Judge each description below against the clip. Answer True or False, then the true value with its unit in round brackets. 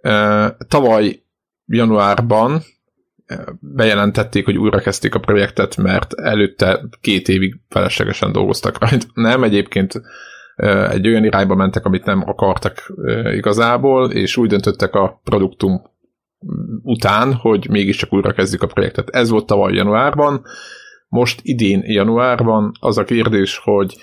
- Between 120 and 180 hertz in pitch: False (105 Hz)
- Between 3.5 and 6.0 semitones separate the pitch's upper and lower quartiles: False (2.9 semitones)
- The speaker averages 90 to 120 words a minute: True (115 wpm)